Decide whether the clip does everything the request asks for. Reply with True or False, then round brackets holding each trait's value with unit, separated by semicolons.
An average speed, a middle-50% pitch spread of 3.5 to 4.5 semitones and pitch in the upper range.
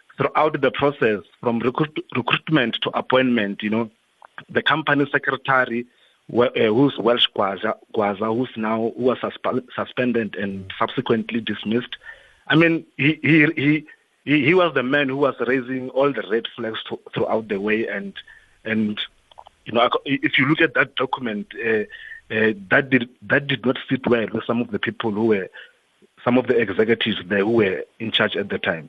False (175 wpm; 4.1 semitones; 130 Hz)